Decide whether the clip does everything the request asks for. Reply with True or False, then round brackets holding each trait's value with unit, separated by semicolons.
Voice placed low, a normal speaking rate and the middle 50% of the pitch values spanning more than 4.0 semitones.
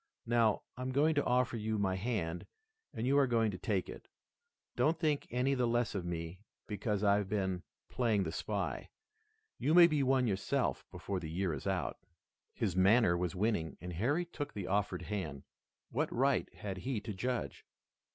True (105 Hz; 180 wpm; 5.1 semitones)